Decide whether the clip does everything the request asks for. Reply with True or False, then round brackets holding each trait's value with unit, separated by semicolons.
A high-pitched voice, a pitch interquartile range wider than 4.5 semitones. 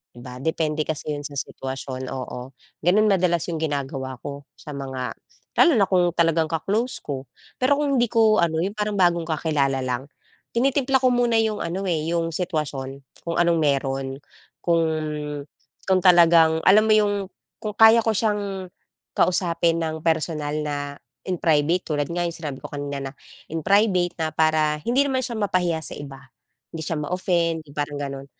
False (165 Hz; 4.9 semitones)